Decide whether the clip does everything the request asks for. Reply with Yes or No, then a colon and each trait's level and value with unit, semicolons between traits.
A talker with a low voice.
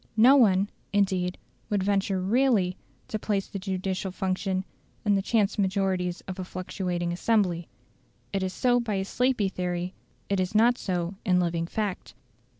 No: high, 190 Hz